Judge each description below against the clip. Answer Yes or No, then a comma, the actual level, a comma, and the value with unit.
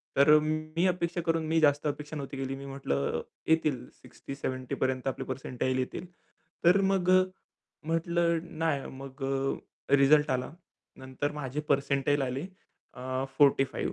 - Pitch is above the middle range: No, medium, 140 Hz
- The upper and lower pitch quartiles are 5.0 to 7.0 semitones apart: No, average, 3.2 semitones